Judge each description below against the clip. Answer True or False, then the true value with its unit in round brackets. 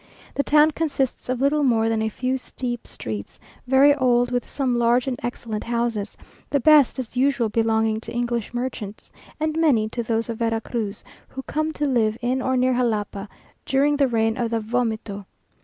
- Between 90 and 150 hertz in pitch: False (240 Hz)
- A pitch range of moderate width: True (3.0 semitones)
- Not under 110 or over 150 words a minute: False (185 wpm)